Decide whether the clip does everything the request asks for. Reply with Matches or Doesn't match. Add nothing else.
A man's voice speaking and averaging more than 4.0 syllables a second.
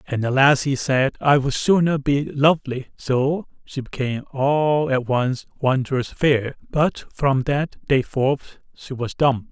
Doesn't match